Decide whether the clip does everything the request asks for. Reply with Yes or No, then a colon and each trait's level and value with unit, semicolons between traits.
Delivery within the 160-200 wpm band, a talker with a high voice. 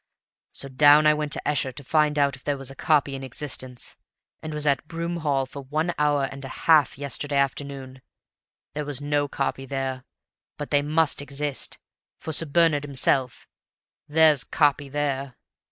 No: average, 170 wpm; medium, 145 Hz